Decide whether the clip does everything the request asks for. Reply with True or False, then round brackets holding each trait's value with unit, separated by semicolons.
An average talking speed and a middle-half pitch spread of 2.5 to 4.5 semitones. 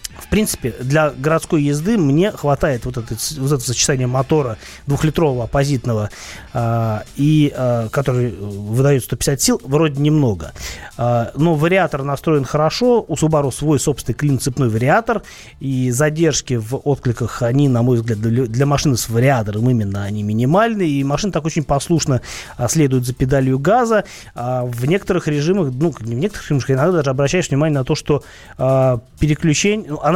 True (145 wpm; 4.1 semitones)